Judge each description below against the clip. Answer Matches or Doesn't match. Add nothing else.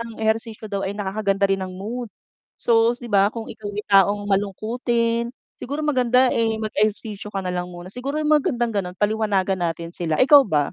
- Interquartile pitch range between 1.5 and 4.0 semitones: Matches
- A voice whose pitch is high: Matches